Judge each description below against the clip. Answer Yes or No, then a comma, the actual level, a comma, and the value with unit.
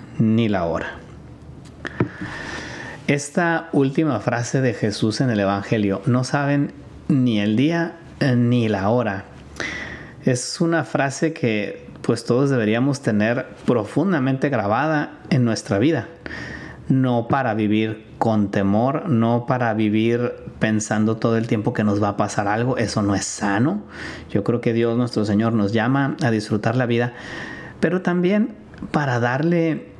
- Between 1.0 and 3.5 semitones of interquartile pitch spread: No, average, 4.4 semitones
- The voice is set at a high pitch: No, low, 120 Hz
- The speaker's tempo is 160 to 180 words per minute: No, average, 140 wpm